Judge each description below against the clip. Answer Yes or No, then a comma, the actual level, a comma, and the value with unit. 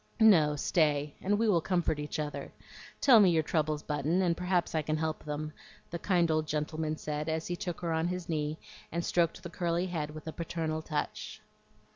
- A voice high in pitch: No, medium, 160 Hz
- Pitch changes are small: Yes, narrow, 2.3 semitones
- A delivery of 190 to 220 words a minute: Yes, average, 200 wpm